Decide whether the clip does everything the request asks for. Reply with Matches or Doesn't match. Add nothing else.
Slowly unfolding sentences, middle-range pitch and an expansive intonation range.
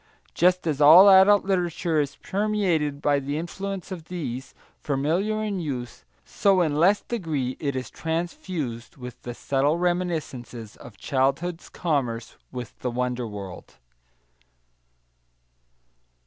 Matches